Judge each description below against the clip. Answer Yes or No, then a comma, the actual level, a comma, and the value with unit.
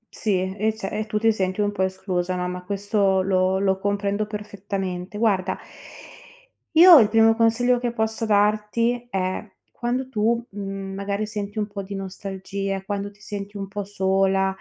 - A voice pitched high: Yes, high, 200 Hz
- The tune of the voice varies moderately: No, narrow, 2.0 semitones